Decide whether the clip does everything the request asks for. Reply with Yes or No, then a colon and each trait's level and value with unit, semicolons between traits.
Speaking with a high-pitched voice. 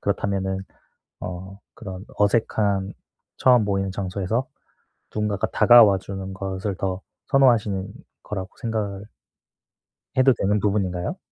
No: low, 100 Hz